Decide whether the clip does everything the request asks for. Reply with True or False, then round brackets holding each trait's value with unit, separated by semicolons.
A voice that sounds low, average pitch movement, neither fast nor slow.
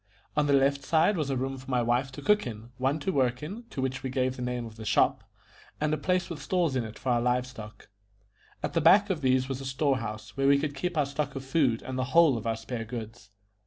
False (130 Hz; 3.3 semitones; 270 wpm)